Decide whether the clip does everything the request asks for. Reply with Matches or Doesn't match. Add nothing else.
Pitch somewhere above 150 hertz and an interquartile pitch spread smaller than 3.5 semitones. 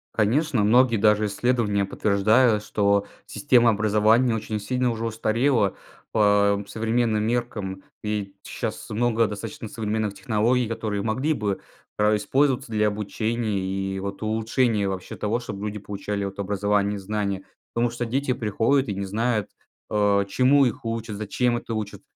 Doesn't match